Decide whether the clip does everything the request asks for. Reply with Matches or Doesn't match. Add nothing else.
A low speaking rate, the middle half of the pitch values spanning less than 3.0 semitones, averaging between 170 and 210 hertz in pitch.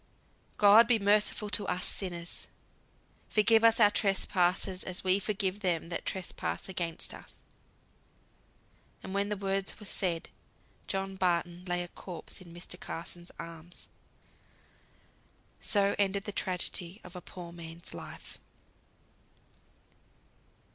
Matches